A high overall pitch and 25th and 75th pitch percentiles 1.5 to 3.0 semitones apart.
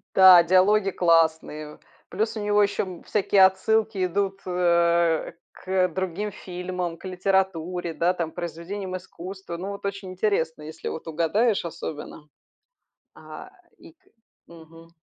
No: medium, 180 Hz; narrow, 2.6 semitones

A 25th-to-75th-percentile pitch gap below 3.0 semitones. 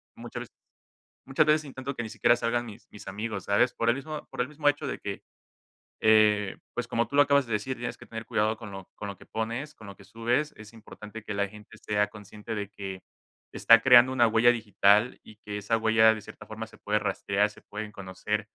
Yes: narrow, 2.6 semitones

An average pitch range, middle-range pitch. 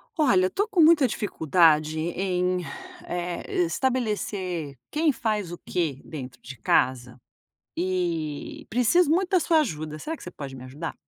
No: wide, 8.2 semitones; medium, 180 Hz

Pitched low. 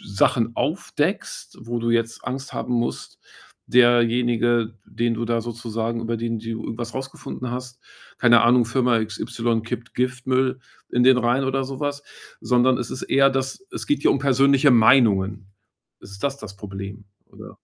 Yes: low, 120 Hz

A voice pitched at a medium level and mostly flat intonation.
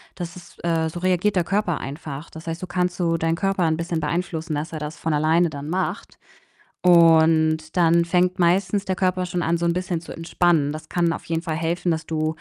Yes: medium, 170 Hz; narrow, 1.9 semitones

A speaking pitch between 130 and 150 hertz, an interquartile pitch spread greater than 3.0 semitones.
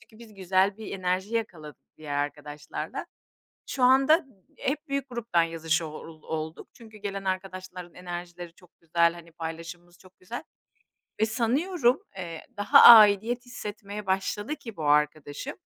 No: medium, 185 Hz; average, 5.2 semitones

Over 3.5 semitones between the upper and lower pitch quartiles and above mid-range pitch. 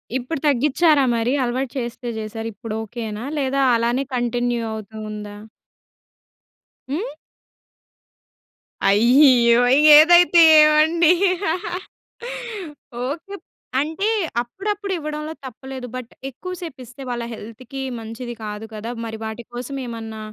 Yes: average, 4.8 semitones; high, 245 Hz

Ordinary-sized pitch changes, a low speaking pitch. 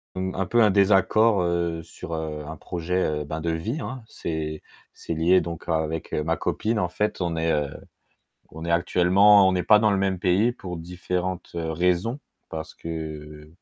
Yes: average, 3.1 semitones; very low, 85 Hz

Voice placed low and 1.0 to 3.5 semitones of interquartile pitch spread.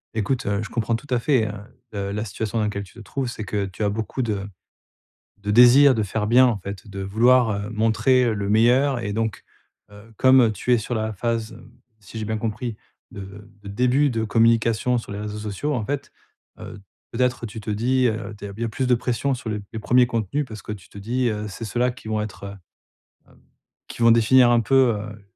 Yes: low, 110 Hz; average, 2.8 semitones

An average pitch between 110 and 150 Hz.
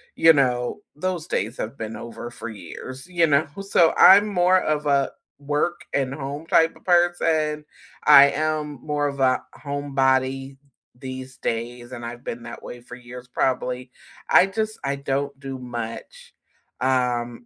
Yes: low, 135 Hz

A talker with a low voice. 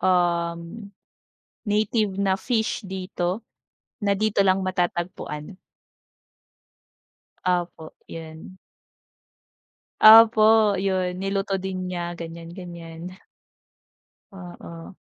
No: medium, 185 Hz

